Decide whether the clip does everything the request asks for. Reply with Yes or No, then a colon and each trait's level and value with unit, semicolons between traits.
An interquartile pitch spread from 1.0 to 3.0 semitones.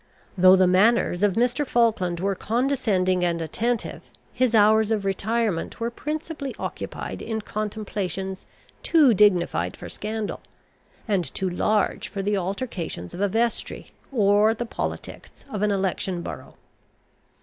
No: average, 3.7 semitones